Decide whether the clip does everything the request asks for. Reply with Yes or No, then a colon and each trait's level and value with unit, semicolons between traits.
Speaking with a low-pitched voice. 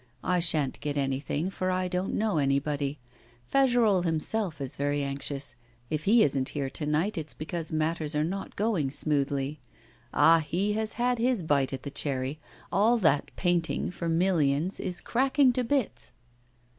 No: medium, 160 Hz